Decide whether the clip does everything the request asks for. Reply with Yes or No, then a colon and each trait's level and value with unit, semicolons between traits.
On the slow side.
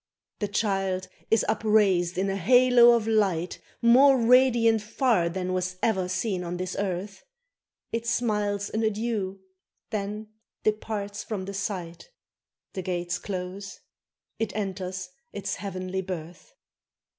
Yes: slow, 125 wpm